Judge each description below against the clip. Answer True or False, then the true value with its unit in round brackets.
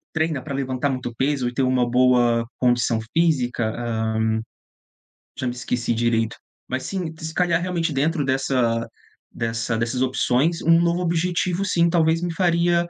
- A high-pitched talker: False (135 Hz)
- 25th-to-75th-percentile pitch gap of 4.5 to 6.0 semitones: True (5.5 semitones)